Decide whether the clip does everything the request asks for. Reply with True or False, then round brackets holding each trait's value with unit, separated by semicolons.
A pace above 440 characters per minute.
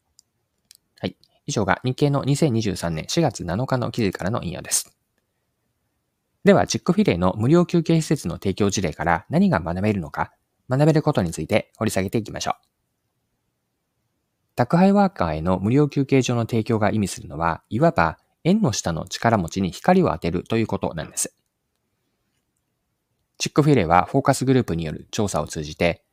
False (335 characters per minute)